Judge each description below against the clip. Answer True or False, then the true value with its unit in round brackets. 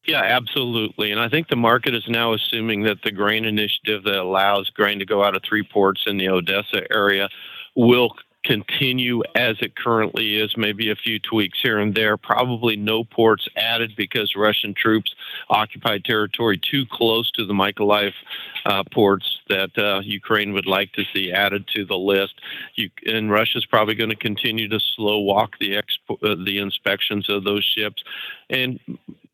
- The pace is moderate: True (180 wpm)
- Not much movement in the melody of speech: True (2.2 semitones)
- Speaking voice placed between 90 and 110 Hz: True (105 Hz)